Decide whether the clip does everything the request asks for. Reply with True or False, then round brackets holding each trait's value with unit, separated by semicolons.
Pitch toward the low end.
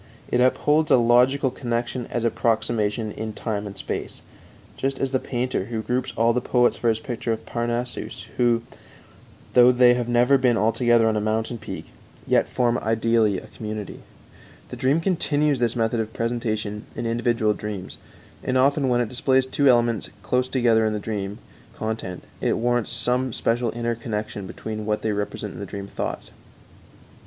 True (120 Hz)